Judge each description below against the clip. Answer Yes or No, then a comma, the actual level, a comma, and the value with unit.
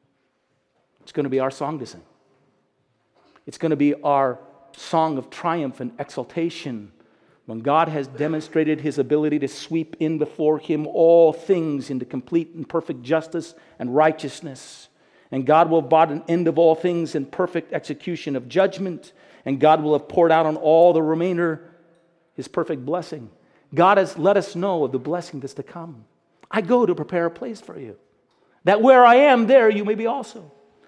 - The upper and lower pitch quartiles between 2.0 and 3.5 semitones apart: Yes, average, 2.9 semitones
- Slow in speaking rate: No, average, 185 wpm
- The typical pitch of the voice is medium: Yes, medium, 160 Hz